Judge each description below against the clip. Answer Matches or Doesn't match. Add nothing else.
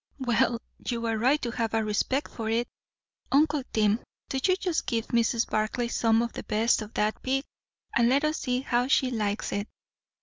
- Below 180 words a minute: Doesn't match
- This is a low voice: Doesn't match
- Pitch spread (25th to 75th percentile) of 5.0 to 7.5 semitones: Doesn't match